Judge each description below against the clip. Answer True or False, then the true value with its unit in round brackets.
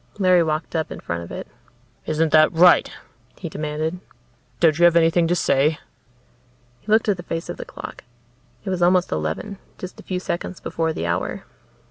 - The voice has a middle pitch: True (165 Hz)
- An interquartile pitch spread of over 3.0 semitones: False (2.6 semitones)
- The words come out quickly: False (185 wpm)